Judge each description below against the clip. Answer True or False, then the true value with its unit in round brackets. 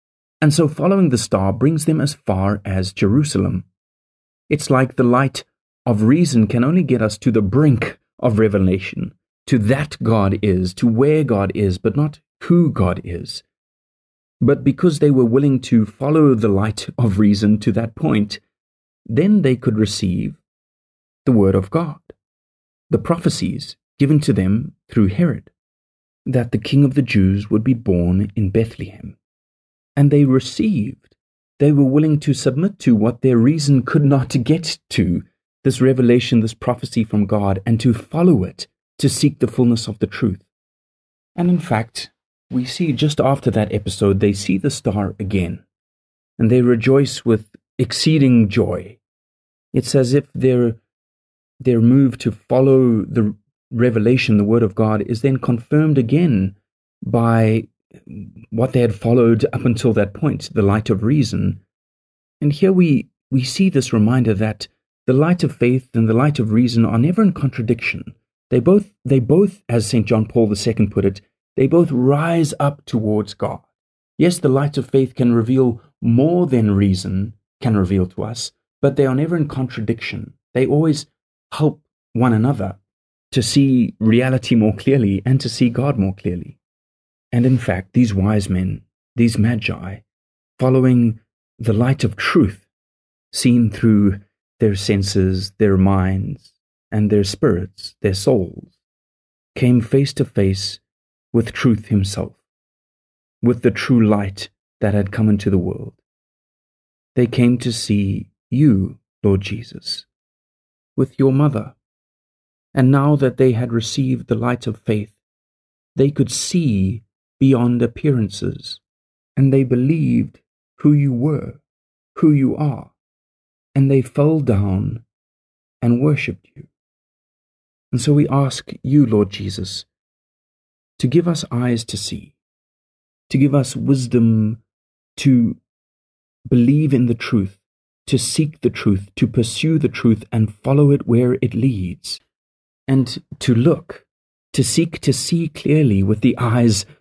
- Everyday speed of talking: True (150 wpm)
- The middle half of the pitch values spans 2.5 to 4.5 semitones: False (5.1 semitones)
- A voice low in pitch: True (120 Hz)